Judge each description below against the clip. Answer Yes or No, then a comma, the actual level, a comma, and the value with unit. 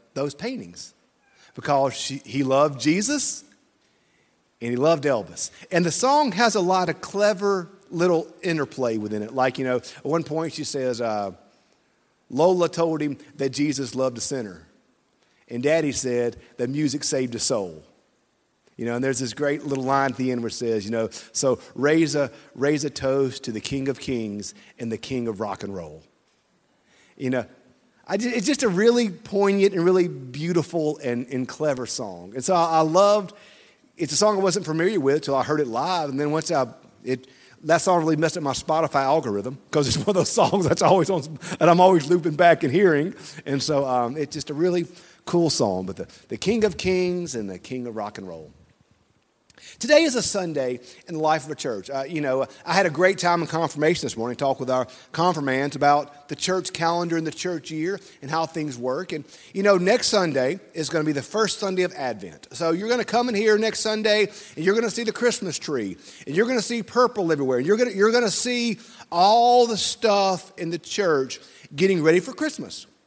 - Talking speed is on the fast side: Yes, fast, 210 wpm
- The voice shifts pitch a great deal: Yes, wide, 5.9 semitones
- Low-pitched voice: No, medium, 155 Hz